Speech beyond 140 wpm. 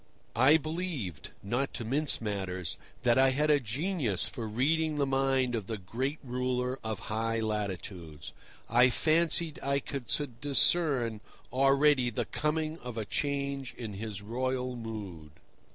No: slow, 135 wpm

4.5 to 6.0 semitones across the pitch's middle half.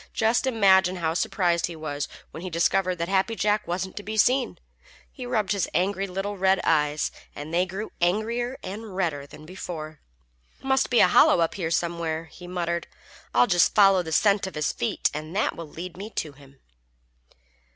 No: average, 3.7 semitones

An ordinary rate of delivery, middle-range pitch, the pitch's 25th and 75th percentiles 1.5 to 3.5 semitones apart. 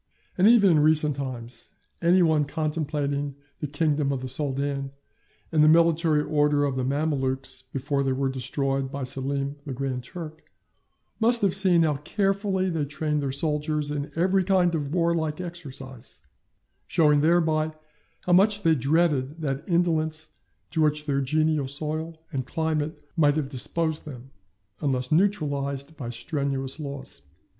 Yes: average, 150 wpm; medium, 150 Hz; average, 2.9 semitones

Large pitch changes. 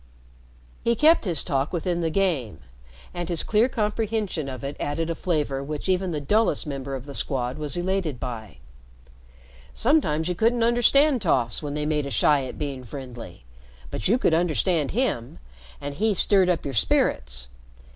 Yes: wide, 6.2 semitones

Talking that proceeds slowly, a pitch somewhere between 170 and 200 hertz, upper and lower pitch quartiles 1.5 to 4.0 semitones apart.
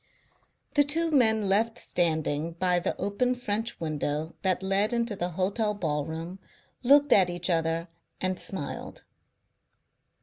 No: slow, 130 wpm; high, 190 Hz; average, 5.2 semitones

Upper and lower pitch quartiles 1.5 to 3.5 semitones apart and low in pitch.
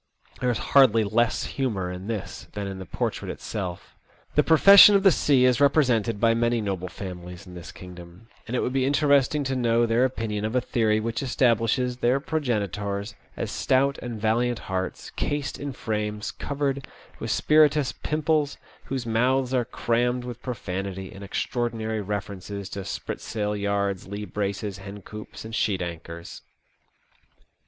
No: average, 4.3 semitones; low, 115 Hz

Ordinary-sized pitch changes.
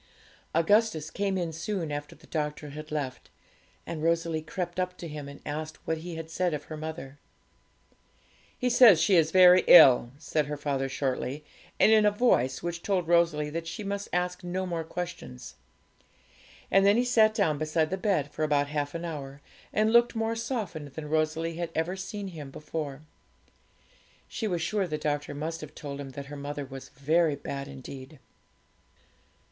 Yes: average, 3.7 semitones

